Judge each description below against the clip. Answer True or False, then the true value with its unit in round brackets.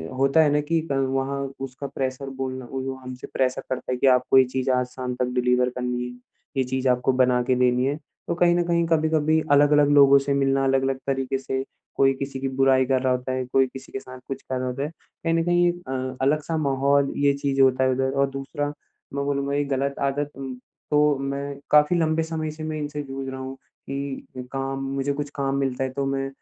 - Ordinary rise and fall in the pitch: False (1.7 semitones)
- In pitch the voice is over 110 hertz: True (135 Hz)